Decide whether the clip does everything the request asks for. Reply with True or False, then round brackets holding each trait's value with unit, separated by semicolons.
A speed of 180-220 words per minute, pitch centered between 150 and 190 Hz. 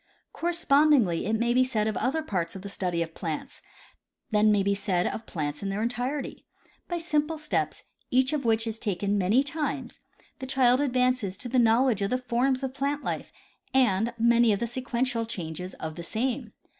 False (195 wpm; 235 Hz)